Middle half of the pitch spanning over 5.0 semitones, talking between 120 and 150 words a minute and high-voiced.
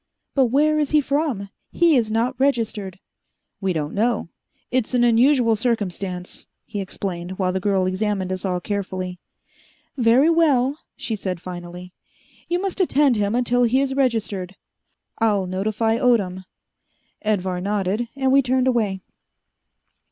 Yes: wide, 5.4 semitones; average, 140 wpm; high, 220 Hz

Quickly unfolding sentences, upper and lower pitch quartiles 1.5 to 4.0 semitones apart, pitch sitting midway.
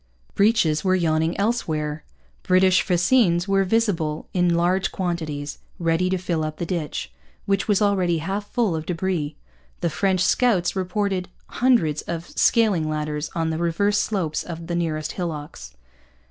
No: average, 145 wpm; average, 3.6 semitones; medium, 175 Hz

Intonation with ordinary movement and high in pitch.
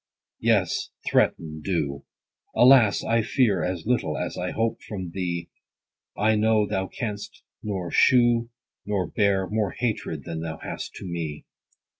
No: average, 4.6 semitones; low, 100 Hz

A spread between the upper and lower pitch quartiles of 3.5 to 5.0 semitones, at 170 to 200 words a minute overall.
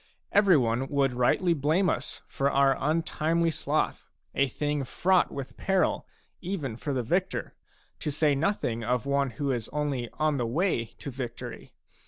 No: average, 4.1 semitones; average, 160 wpm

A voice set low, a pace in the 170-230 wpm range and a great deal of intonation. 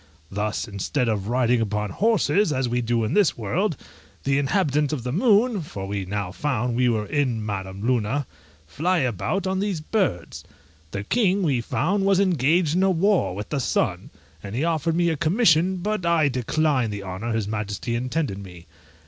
Yes: low, 130 Hz; average, 180 wpm; wide, 8.4 semitones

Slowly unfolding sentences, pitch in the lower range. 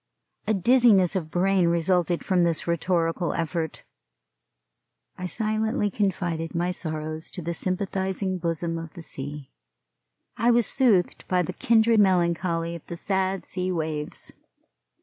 No: slow, 130 wpm; medium, 180 Hz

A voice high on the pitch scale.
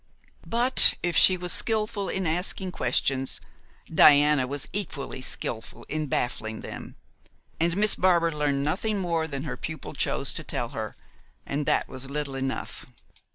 No: medium, 155 Hz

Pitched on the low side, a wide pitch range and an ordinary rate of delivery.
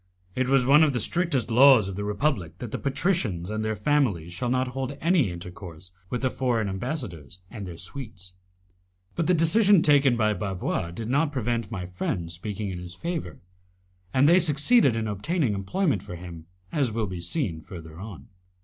Yes: low, 115 Hz; wide, 7.3 semitones; average, 185 wpm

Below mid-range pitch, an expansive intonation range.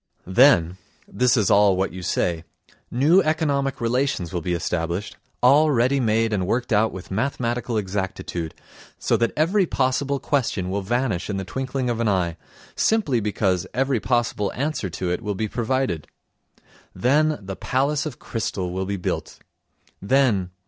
Yes: low, 115 Hz; wide, 6.0 semitones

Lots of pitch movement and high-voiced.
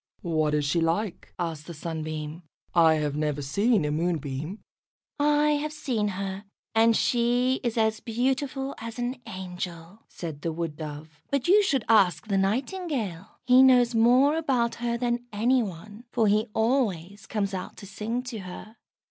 Yes: wide, 6.6 semitones; high, 210 Hz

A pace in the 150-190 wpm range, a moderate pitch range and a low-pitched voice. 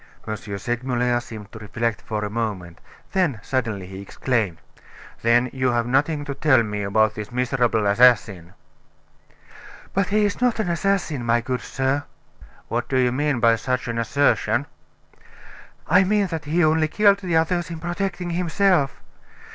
No: average, 155 wpm; wide, 6.4 semitones; low, 130 Hz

